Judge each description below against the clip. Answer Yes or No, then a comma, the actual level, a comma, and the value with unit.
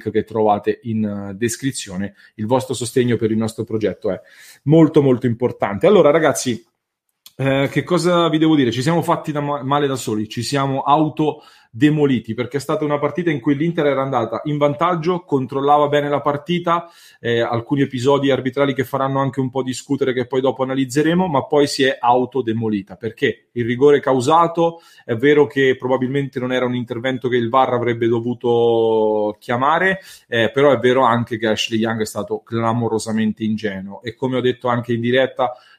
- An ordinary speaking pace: Yes, average, 180 wpm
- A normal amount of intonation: Yes, average, 3.8 semitones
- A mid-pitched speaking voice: No, low, 130 Hz